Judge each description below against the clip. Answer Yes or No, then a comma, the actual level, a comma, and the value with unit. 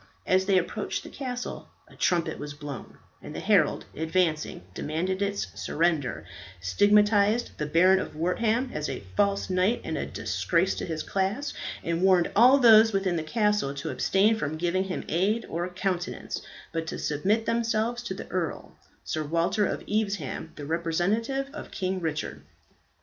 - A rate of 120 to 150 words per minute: No, average, 160 wpm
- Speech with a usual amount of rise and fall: Yes, average, 4.6 semitones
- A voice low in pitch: No, medium, 185 Hz